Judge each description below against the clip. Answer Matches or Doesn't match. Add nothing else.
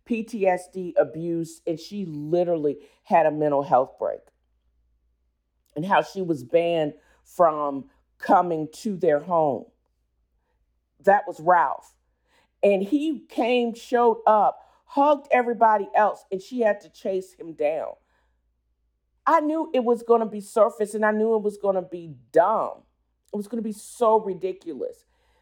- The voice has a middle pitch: Matches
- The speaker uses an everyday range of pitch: Doesn't match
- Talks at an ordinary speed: Matches